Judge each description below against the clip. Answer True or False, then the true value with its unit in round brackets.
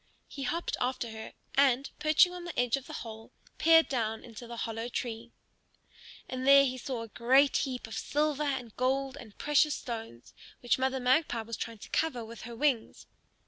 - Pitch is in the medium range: False (250 Hz)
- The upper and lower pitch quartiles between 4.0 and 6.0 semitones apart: False (3.3 semitones)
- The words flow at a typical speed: True (185 wpm)